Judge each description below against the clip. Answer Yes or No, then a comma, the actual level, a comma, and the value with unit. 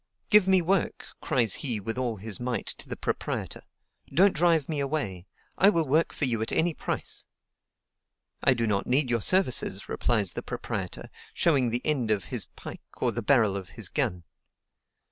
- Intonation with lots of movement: Yes, wide, 6.5 semitones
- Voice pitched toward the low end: Yes, low, 125 Hz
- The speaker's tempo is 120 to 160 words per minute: No, average, 180 wpm